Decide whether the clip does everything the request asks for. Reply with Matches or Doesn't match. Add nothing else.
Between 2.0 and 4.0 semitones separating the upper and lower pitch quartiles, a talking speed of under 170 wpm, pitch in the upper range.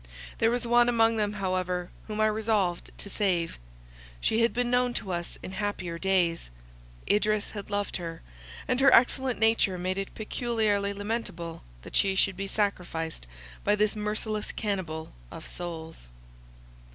Matches